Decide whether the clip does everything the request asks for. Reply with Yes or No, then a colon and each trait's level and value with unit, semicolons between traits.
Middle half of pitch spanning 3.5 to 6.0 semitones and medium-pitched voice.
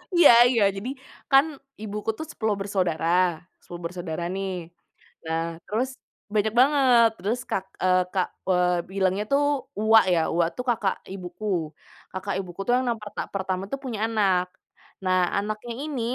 No: average, 3.9 semitones; high, 200 Hz